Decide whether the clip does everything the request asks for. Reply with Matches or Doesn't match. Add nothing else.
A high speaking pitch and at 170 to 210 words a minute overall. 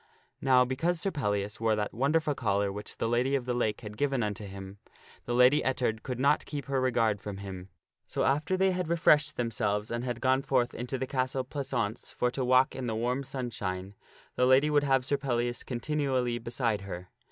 Doesn't match